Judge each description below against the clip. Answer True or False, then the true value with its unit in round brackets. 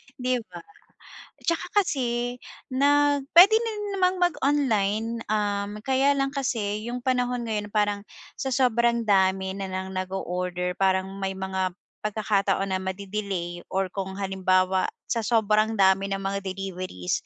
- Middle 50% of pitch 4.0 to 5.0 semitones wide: True (4.3 semitones)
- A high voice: True (205 Hz)